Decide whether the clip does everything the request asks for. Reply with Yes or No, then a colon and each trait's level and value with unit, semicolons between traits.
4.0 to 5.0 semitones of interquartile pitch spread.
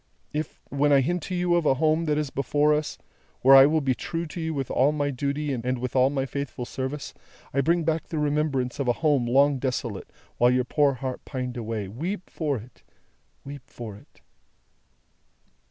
No: average, 3.1 semitones